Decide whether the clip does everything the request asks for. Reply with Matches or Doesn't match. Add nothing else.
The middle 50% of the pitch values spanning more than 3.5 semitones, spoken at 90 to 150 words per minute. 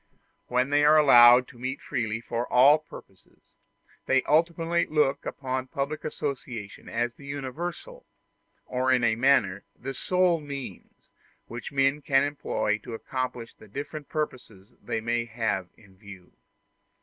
Matches